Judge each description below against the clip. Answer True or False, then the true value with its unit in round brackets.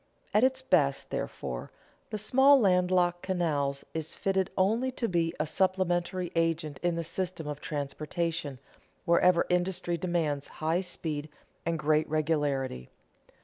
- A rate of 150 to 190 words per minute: False (135 wpm)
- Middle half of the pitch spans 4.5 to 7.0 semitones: False (3.3 semitones)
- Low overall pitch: False (170 Hz)